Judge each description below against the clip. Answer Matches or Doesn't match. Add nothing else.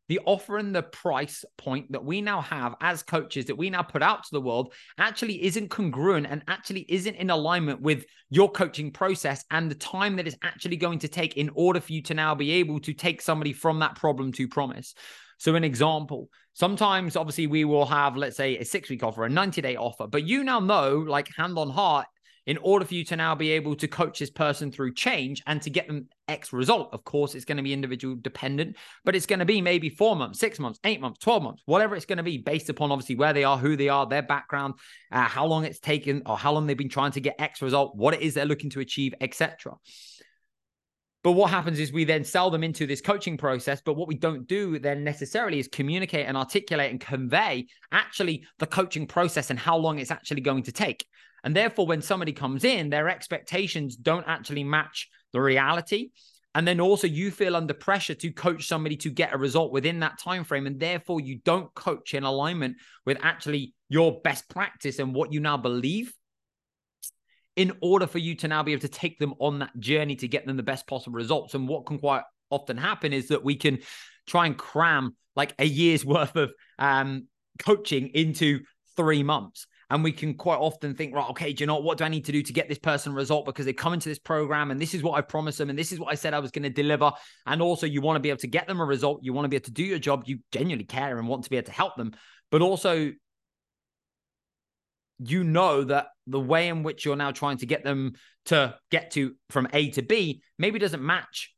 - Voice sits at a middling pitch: Matches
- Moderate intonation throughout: Matches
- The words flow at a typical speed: Doesn't match